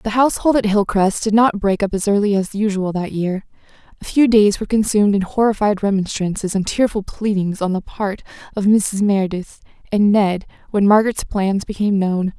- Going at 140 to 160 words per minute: No, average, 185 wpm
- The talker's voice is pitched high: Yes, high, 205 Hz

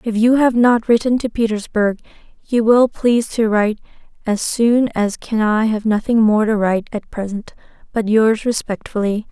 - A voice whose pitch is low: No, high, 220 Hz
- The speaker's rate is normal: Yes, average, 175 wpm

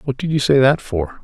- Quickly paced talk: Yes, fast, 290 wpm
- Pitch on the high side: No, low, 130 Hz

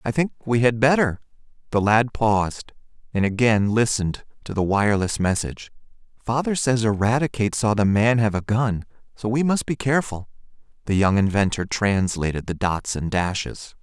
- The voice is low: Yes, low, 110 Hz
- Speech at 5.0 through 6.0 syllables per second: Yes, 5.3 syllables/s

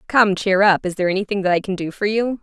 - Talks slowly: No, fast, 295 wpm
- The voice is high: Yes, high, 195 Hz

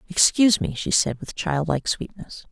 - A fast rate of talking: No, average, 165 wpm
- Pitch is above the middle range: No, medium, 165 Hz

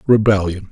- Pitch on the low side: Yes, low, 100 Hz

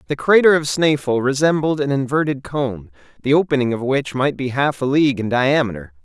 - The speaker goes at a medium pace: Yes, average, 190 wpm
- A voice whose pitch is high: No, low, 135 Hz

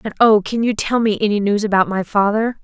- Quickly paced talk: Yes, fast, 250 wpm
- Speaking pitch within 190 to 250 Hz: Yes, high, 210 Hz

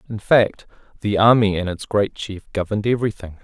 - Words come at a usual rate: Yes, average, 175 wpm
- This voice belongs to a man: Yes, male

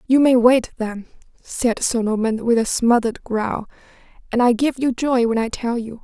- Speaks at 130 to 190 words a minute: No, average, 200 wpm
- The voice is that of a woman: Yes, female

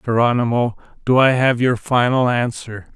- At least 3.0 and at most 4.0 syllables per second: No, 4.7 syllables/s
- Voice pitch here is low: Yes, low, 120 Hz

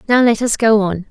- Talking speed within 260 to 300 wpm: Yes, fast, 270 wpm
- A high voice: Yes, high, 220 Hz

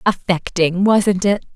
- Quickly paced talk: No, slow, 115 wpm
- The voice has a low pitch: No, high, 190 Hz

